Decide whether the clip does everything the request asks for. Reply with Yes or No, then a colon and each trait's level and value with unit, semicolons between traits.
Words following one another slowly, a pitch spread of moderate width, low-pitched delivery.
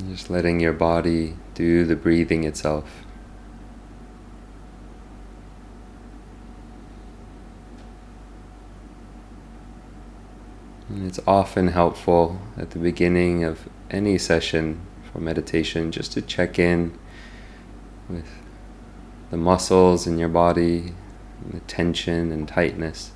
No: slow, 90 wpm; narrow, 2.0 semitones; very low, 85 Hz